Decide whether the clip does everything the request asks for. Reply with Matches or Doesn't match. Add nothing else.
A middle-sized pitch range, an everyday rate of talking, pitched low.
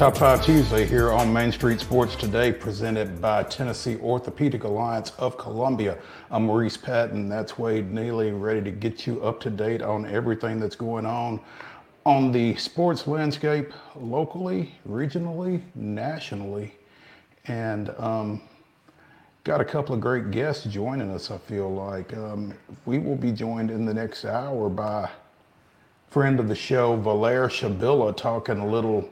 Matches